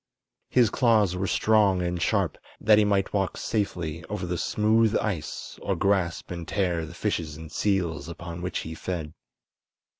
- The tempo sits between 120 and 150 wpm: No, average, 160 wpm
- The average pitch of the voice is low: Yes, very low, 90 Hz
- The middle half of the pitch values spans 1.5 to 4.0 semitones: Yes, average, 3.7 semitones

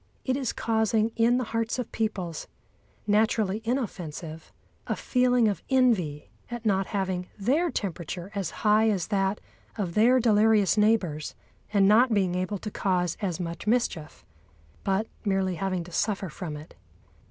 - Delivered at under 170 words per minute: Yes, average, 150 wpm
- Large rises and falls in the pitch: No, average, 3.7 semitones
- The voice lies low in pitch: No, high, 205 Hz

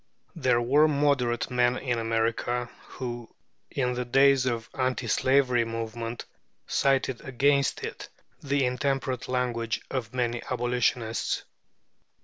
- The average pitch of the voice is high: No, low, 125 Hz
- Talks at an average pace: No, slow, 120 wpm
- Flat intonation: Yes, narrow, 2.0 semitones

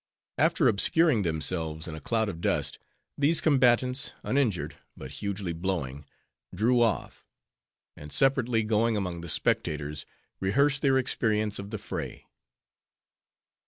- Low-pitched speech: Yes, low, 105 Hz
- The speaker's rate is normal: No, slow, 125 wpm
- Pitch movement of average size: No, wide, 6.8 semitones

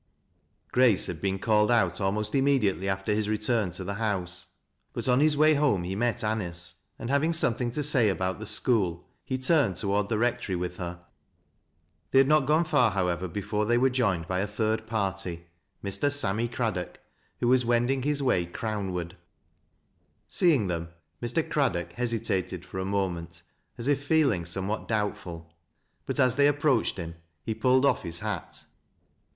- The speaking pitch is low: Yes, low, 105 Hz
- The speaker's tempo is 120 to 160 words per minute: No, average, 175 wpm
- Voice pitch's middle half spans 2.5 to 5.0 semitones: No, wide, 5.5 semitones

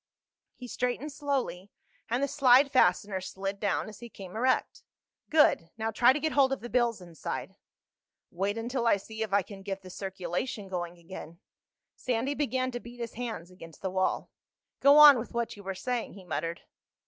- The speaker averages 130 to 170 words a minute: No, average, 185 wpm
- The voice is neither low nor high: No, high, 225 Hz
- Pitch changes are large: No, average, 5.0 semitones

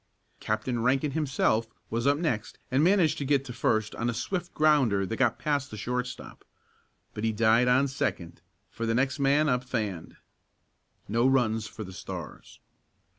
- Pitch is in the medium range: No, low, 125 Hz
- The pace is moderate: Yes, average, 170 wpm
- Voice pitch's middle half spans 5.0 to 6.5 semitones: No, average, 4.0 semitones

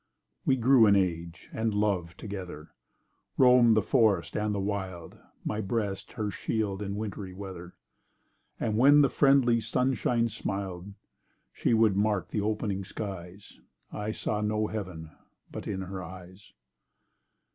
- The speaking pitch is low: Yes, low, 105 Hz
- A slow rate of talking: Yes, slow, 130 wpm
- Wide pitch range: No, average, 2.8 semitones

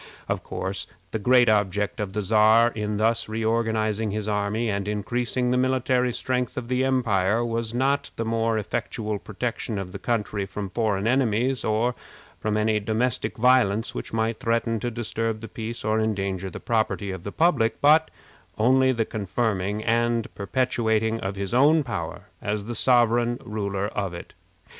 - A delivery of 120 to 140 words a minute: No, average, 160 wpm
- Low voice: Yes, low, 110 Hz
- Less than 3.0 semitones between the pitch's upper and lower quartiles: Yes, narrow, 2.5 semitones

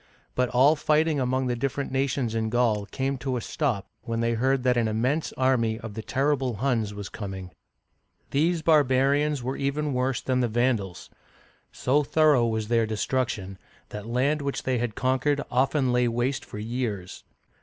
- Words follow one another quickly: No, average, 170 wpm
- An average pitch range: Yes, average, 3.3 semitones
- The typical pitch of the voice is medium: No, low, 125 Hz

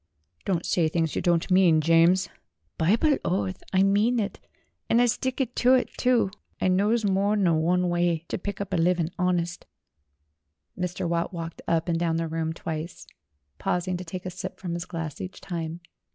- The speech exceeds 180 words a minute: Yes, average, 190 wpm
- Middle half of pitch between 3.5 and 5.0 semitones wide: No, average, 2.7 semitones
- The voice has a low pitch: No, medium, 180 Hz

